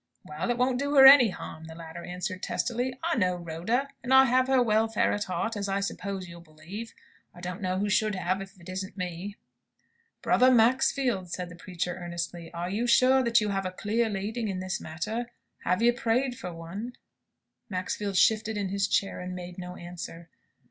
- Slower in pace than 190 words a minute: No, average, 195 wpm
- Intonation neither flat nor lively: Yes, average, 4.7 semitones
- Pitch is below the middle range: No, high, 195 Hz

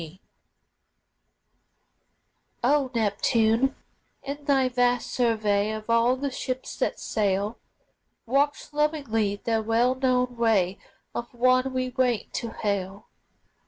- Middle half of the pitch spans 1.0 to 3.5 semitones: Yes, average, 3.1 semitones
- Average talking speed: No, slow, 110 wpm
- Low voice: No, high, 240 Hz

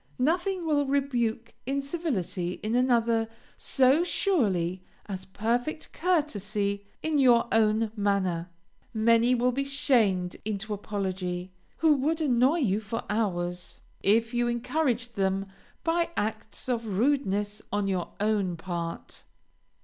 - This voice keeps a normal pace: No, slow, 120 wpm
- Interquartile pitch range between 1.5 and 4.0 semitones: No, wide, 5.4 semitones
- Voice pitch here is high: Yes, high, 225 Hz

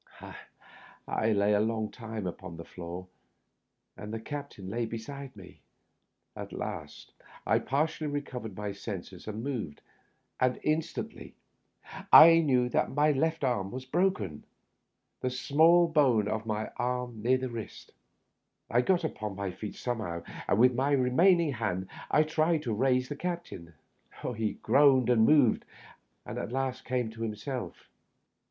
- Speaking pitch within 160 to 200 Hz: No, low, 125 Hz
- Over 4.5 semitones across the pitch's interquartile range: Yes, average, 5.0 semitones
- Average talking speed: Yes, average, 150 wpm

